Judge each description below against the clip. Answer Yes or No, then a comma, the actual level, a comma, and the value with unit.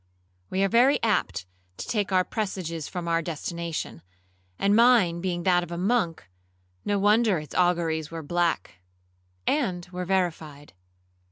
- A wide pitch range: No, average, 3.4 semitones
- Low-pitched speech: No, medium, 175 Hz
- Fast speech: No, average, 140 wpm